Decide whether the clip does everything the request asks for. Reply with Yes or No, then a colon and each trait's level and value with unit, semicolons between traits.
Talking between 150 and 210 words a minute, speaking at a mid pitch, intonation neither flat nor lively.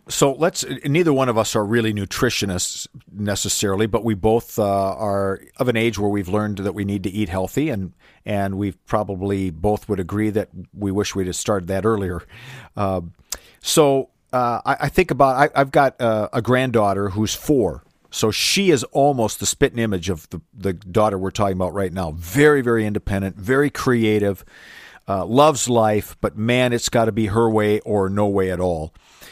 No: average, 190 wpm; low, 105 Hz; average, 3.4 semitones